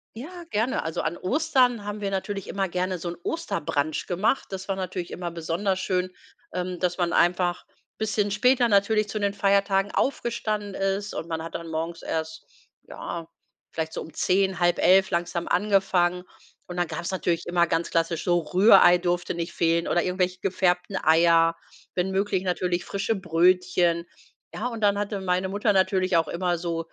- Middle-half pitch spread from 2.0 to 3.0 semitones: Yes, narrow, 2.6 semitones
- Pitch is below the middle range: No, medium, 185 Hz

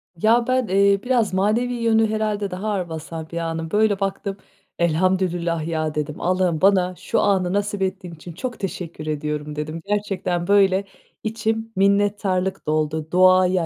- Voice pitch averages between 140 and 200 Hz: Yes, medium, 185 Hz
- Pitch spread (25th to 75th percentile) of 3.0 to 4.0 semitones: Yes, average, 3.6 semitones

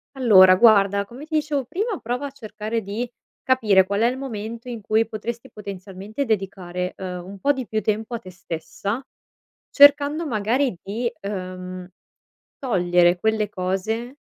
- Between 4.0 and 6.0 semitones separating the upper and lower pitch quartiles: Yes, average, 4.5 semitones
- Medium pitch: No, high, 215 Hz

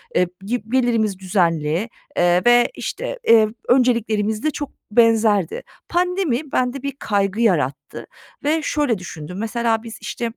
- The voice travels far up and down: No, average, 4.2 semitones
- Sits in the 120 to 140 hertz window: No, high, 225 Hz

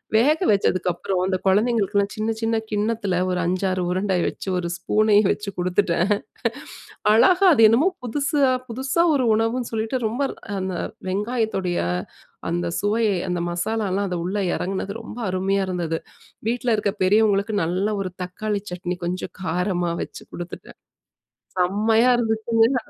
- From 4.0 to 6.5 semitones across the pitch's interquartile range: No, average, 3.6 semitones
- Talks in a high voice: Yes, high, 205 Hz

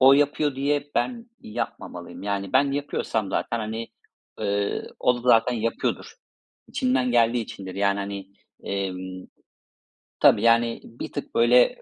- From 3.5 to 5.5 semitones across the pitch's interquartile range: Yes, average, 4.6 semitones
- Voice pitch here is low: Yes, low, 115 Hz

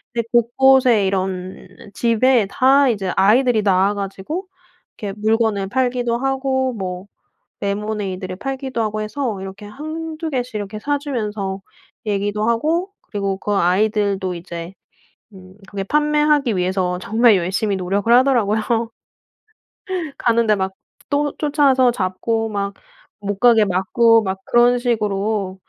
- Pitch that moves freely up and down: No, average, 4.4 semitones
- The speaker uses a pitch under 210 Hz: No, high, 215 Hz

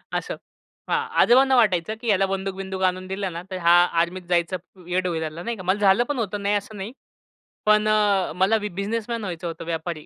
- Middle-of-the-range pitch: No, high, 195 Hz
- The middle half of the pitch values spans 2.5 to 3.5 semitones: Yes, average, 2.9 semitones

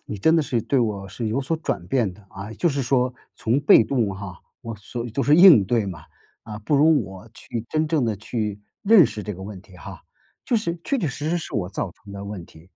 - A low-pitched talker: Yes, low, 115 Hz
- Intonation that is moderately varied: No, wide, 6.3 semitones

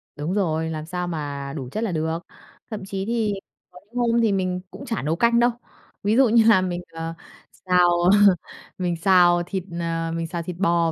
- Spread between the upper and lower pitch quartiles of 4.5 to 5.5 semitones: No, average, 3.7 semitones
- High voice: No, medium, 180 Hz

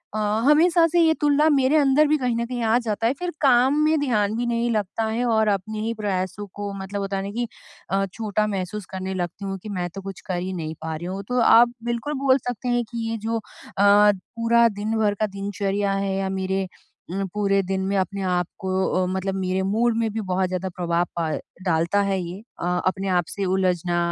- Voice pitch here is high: Yes, high, 200 Hz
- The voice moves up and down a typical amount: Yes, average, 3.8 semitones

